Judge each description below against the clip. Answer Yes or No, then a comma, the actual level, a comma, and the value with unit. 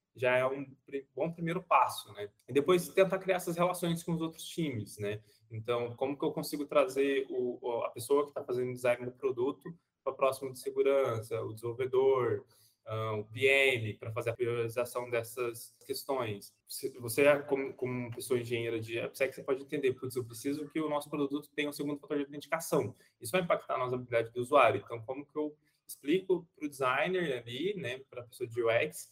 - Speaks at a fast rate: Yes, fast, 195 wpm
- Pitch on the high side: No, low, 135 Hz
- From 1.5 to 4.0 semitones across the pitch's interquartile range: No, average, 5.1 semitones